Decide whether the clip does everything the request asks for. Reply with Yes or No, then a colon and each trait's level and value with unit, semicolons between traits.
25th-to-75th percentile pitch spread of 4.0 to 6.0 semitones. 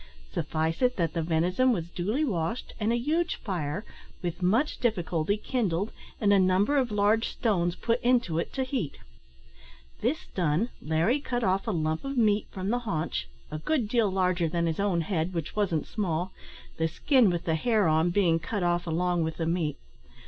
Yes: wide, 5.5 semitones